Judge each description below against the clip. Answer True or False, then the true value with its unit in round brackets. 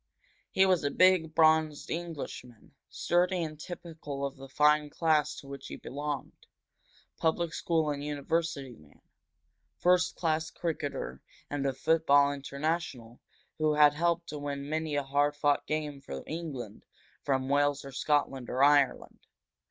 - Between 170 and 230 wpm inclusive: False (145 wpm)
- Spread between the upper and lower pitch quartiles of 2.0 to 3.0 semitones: True (2.5 semitones)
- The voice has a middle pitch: True (150 Hz)